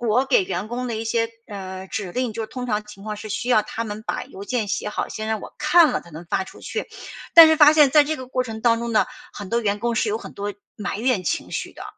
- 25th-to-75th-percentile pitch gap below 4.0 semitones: Yes, average, 3.4 semitones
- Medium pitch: No, high, 225 Hz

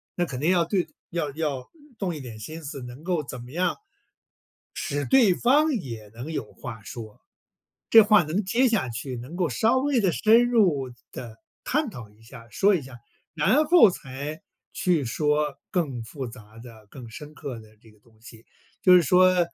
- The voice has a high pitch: No, medium, 150 Hz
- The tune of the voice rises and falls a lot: Yes, wide, 7.1 semitones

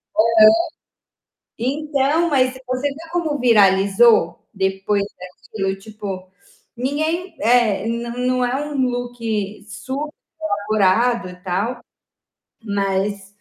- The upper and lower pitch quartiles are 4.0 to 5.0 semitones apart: Yes, average, 4.5 semitones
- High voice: Yes, high, 230 Hz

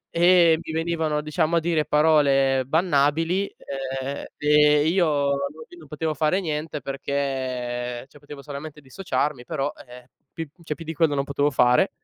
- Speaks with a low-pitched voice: No, medium, 150 Hz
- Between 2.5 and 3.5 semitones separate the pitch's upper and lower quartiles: Yes, average, 2.8 semitones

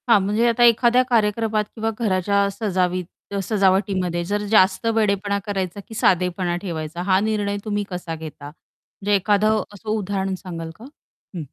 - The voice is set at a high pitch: Yes, high, 200 Hz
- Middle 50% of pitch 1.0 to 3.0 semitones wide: Yes, average, 2.7 semitones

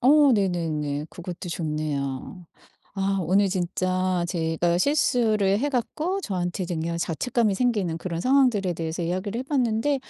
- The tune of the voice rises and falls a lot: Yes, wide, 5.7 semitones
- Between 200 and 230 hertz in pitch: No, medium, 185 Hz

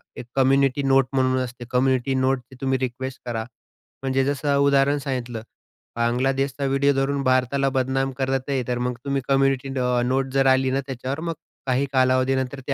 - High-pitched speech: No, low, 135 Hz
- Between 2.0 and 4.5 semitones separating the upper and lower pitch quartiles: No, narrow, 1.1 semitones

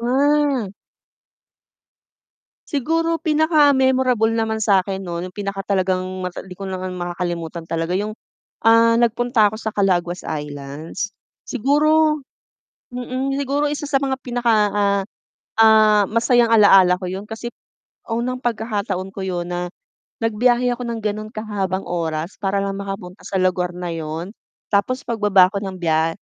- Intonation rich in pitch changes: No, average, 4.8 semitones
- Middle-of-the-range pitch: No, high, 205 Hz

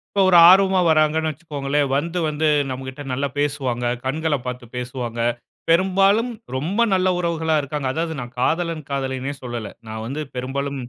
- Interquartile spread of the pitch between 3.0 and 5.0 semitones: Yes, average, 4.0 semitones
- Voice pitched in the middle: Yes, medium, 145 Hz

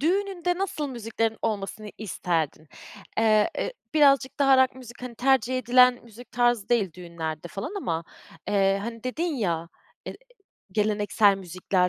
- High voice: Yes, high, 225 Hz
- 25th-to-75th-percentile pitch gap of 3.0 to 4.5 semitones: No, average, 5.0 semitones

